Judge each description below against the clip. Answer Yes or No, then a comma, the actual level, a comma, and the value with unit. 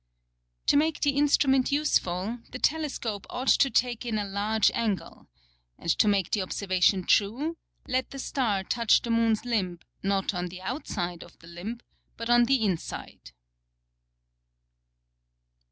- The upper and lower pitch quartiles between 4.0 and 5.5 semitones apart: Yes, average, 4.9 semitones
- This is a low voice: No, high, 220 Hz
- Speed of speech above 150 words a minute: No, average, 145 wpm